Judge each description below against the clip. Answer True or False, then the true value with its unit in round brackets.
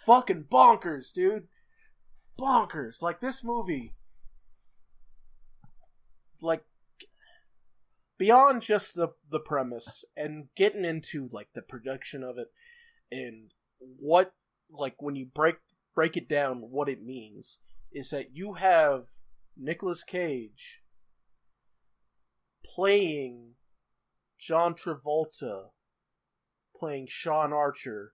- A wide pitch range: True (7.1 semitones)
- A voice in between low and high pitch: True (160 Hz)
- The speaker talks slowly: True (95 wpm)